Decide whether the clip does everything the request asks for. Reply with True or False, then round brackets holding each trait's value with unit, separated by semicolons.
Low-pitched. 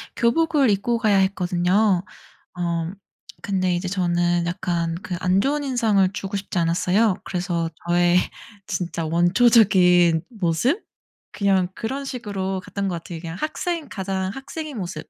False (190 Hz)